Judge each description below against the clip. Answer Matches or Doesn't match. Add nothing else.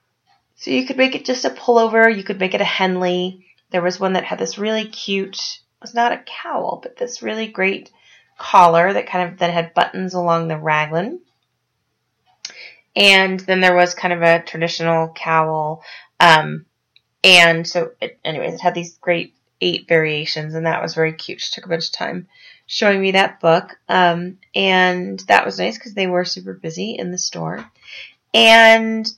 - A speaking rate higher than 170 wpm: Matches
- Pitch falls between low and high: Matches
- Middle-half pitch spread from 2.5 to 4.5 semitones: Matches